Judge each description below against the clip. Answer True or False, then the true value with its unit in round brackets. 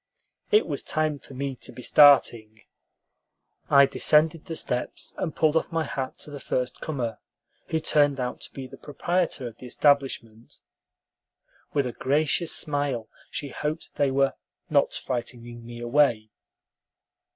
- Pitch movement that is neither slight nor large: True (3.5 semitones)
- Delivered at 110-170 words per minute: True (150 wpm)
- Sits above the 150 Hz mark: False (140 Hz)